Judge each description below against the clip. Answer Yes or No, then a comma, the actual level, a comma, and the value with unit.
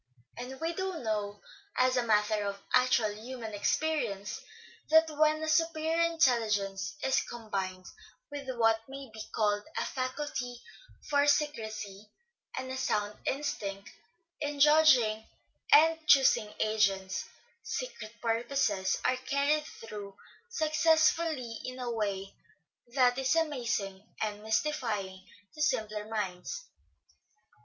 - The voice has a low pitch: No, high, 240 Hz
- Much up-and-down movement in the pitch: Yes, wide, 5.9 semitones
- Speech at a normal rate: No, slow, 115 wpm